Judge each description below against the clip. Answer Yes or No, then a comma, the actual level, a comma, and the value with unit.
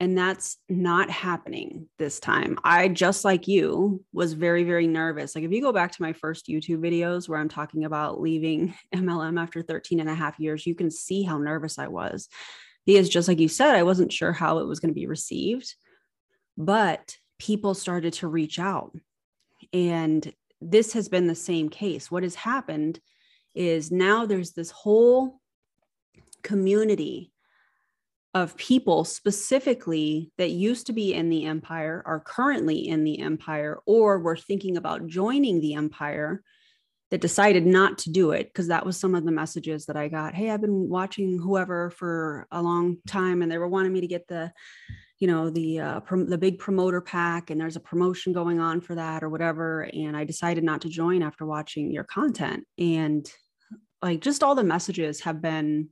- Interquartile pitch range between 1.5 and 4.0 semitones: Yes, average, 3.0 semitones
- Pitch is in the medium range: Yes, medium, 175 Hz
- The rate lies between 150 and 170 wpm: No, average, 185 wpm